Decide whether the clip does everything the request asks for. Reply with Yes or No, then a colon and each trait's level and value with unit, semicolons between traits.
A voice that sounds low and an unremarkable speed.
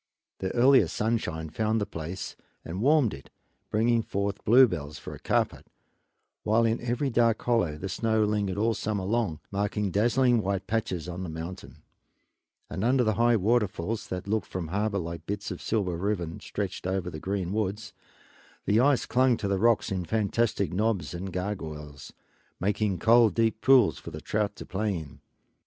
Yes: low, 100 Hz; average, 175 wpm